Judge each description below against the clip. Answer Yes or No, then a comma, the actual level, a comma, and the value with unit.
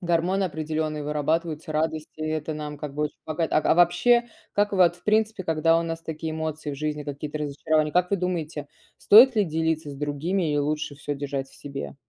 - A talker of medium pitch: Yes, medium, 155 Hz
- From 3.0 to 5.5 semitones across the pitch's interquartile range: No, narrow, 2.4 semitones